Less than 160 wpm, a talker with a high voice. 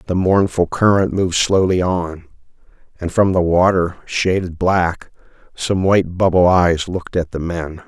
No: average, 150 wpm; very low, 90 Hz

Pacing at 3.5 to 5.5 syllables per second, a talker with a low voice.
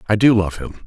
No: 5.9 syllables/s; low, 100 Hz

